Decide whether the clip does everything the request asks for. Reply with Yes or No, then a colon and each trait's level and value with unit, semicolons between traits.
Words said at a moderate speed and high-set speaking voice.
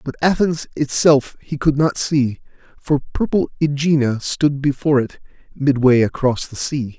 No: average, 145 wpm; medium, 140 Hz